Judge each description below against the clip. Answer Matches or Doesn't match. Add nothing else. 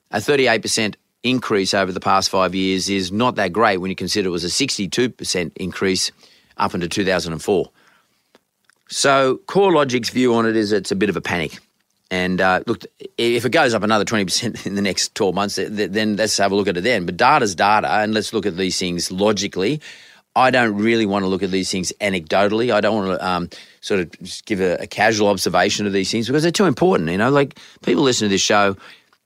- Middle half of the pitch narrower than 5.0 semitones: Matches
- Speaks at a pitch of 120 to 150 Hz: Doesn't match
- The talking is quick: Matches